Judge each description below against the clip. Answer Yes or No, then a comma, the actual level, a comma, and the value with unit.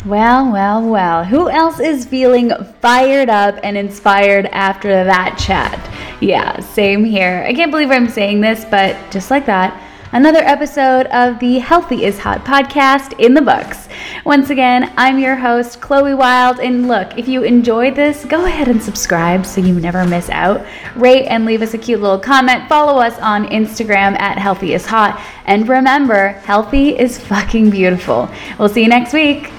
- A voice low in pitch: No, high, 235 Hz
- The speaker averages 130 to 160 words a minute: No, average, 175 wpm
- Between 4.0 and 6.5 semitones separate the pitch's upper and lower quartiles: Yes, average, 4.6 semitones